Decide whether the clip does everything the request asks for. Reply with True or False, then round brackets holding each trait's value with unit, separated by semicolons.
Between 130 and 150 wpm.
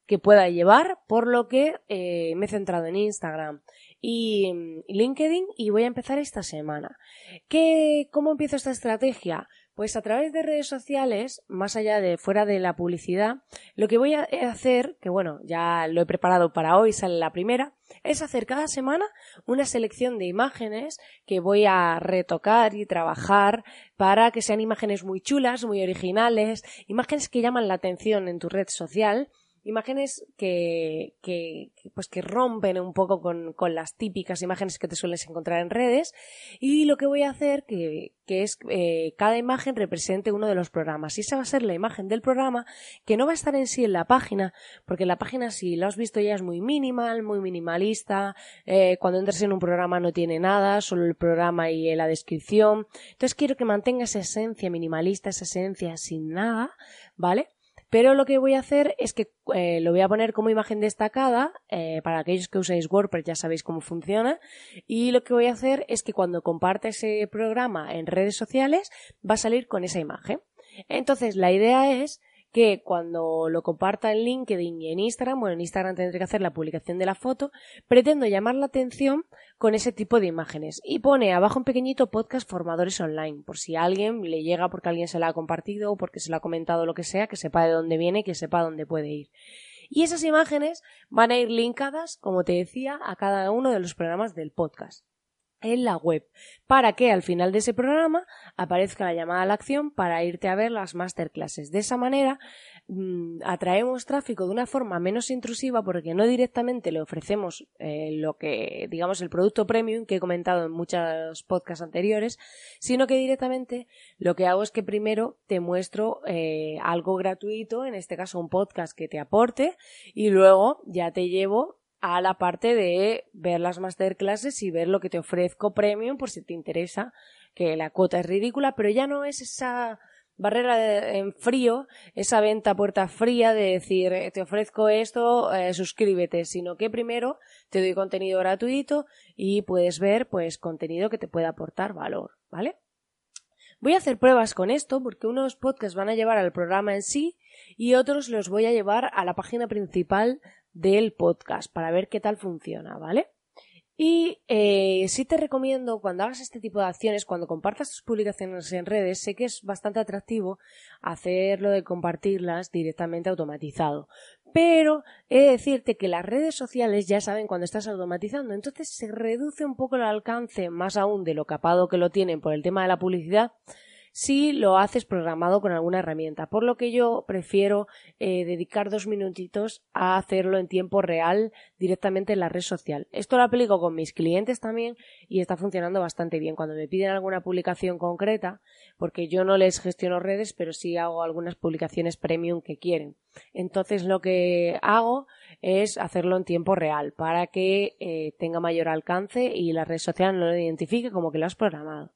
False (190 wpm)